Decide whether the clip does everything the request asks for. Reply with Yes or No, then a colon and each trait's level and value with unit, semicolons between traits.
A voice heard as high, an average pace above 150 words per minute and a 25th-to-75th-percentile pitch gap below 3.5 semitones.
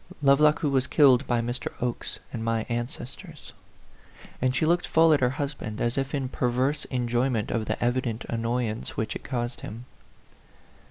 No: low, 125 Hz; average, 170 wpm; average, 2.8 semitones